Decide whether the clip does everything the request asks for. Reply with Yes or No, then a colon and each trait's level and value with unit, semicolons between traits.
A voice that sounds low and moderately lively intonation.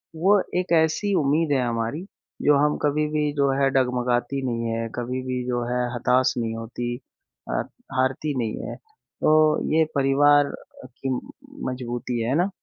Yes: low, 130 Hz; average, 3.6 semitones